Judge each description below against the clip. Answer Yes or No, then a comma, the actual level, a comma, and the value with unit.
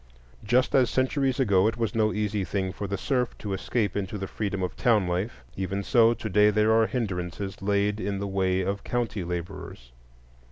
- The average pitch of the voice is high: No, low, 100 Hz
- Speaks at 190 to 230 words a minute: Yes, average, 195 wpm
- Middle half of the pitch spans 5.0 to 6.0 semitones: No, average, 2.9 semitones